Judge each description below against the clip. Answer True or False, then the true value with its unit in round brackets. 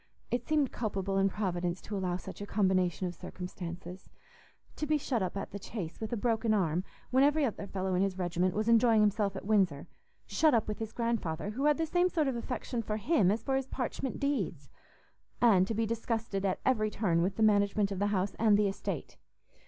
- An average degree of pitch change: True (3.9 semitones)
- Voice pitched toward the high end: True (210 Hz)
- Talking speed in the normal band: False (210 wpm)